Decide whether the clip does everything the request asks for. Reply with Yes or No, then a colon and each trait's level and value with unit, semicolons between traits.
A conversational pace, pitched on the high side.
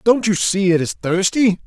No: fast, 215 wpm; high, 200 Hz